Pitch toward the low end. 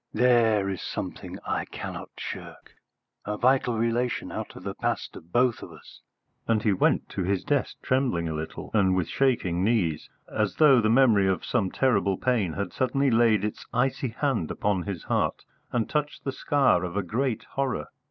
Yes: low, 110 Hz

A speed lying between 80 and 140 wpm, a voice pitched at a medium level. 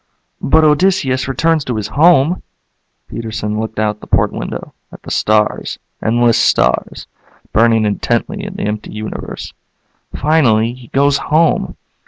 No: slow, 135 wpm; low, 120 Hz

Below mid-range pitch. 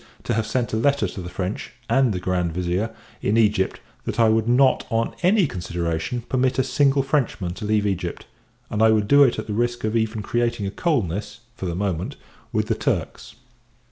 Yes: low, 110 Hz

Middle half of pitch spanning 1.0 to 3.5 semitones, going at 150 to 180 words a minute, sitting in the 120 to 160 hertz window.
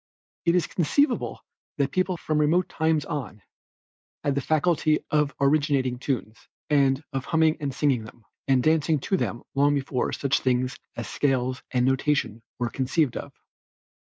Yes: average, 3.2 semitones; average, 155 wpm; medium, 140 Hz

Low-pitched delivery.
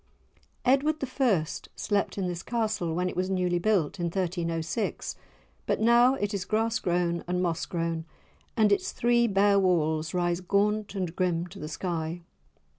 No: medium, 185 Hz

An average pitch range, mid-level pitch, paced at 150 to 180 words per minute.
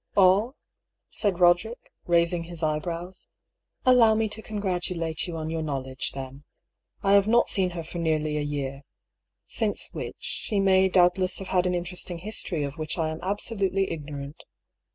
Yes: average, 3.7 semitones; medium, 175 Hz; average, 175 wpm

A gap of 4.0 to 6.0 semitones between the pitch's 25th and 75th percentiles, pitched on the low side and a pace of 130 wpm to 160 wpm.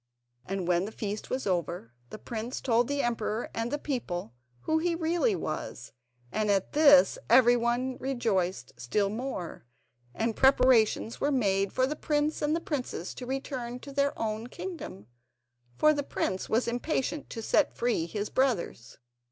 No: average, 5.3 semitones; high, 240 Hz; average, 155 wpm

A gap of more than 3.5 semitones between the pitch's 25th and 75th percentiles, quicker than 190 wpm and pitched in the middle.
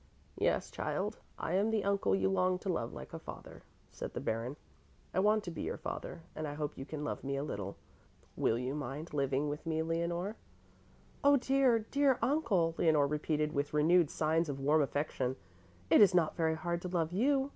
Yes: average, 4.6 semitones; average, 200 wpm; medium, 160 Hz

